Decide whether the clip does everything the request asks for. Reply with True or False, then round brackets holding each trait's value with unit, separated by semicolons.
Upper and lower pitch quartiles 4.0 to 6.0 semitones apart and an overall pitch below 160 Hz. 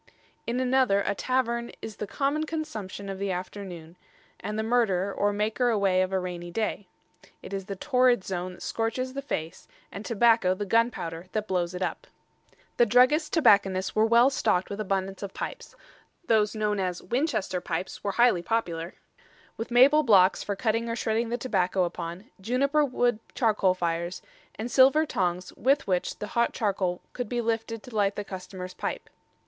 False (4.4 semitones; 210 Hz)